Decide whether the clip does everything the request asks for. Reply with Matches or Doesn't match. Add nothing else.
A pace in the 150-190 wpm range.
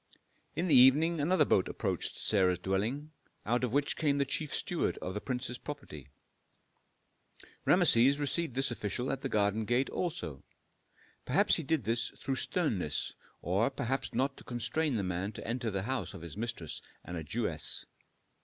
Matches